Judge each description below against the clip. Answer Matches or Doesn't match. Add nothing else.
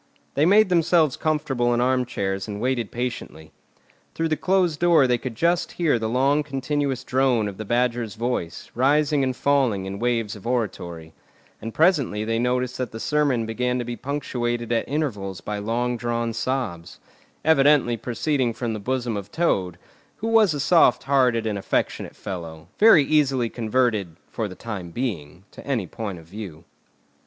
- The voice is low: Matches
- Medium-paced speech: Matches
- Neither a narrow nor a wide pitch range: Matches